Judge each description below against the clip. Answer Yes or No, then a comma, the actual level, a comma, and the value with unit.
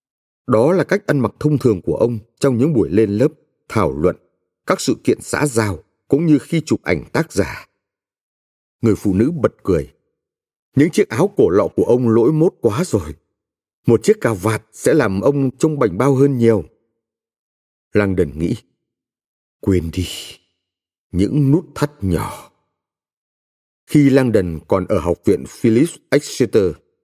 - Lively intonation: Yes, wide, 7.3 semitones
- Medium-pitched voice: No, low, 115 Hz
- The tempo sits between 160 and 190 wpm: Yes, slow, 165 wpm